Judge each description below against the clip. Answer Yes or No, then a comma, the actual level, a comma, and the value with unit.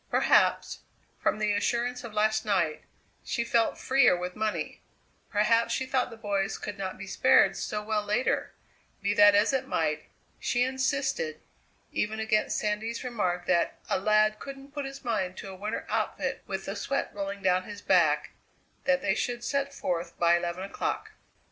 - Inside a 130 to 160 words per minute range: No, average, 170 wpm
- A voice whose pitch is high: Yes, high, 215 Hz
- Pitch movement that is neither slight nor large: Yes, average, 4.0 semitones